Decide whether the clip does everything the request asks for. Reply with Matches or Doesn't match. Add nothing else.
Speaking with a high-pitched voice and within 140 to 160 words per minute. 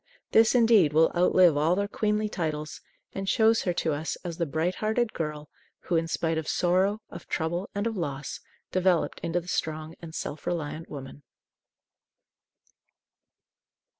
Doesn't match